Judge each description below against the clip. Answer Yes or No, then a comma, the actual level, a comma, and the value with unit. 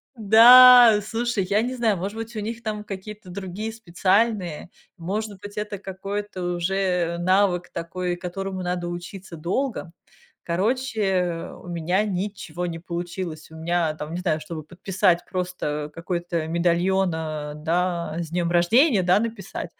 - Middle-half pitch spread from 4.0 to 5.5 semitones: No, average, 3.4 semitones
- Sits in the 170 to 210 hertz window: Yes, medium, 185 Hz